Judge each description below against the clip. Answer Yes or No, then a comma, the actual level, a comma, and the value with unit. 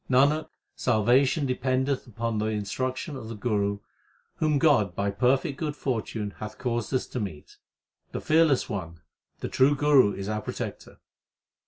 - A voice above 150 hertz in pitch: No, low, 125 Hz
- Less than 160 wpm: Yes, average, 150 wpm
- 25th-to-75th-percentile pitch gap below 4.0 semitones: No, average, 4.5 semitones